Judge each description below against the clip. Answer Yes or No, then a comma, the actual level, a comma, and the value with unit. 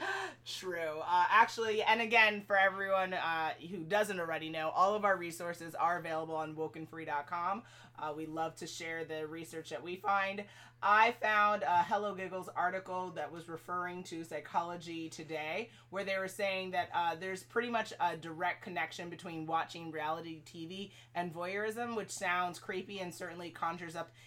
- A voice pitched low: No, medium, 175 Hz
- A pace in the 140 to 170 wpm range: Yes, average, 165 wpm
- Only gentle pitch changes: No, average, 3.1 semitones